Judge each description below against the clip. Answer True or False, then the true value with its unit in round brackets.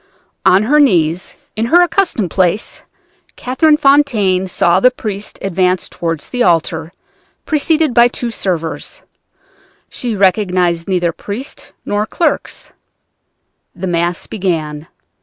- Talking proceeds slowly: True (115 wpm)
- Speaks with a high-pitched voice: True (195 Hz)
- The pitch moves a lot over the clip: True (6.2 semitones)